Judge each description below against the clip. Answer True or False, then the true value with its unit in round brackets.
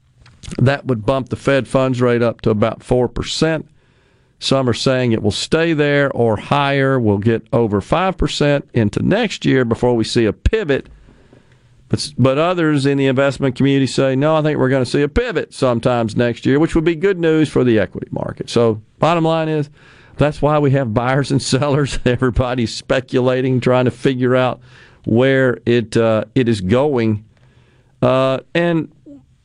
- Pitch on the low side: True (130 Hz)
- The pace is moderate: True (180 wpm)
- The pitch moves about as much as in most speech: True (3.0 semitones)